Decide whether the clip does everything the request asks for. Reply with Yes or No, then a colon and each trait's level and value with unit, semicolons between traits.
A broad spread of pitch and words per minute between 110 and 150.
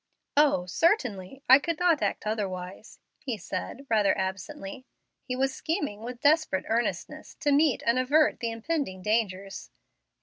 Yes: wide, 6.6 semitones; average, 140 wpm